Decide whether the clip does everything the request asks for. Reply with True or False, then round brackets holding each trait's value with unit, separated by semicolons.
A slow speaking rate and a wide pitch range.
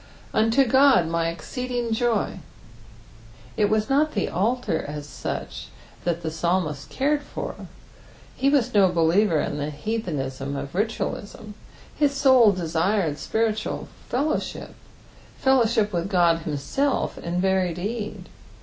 True (120 wpm; 6.3 semitones)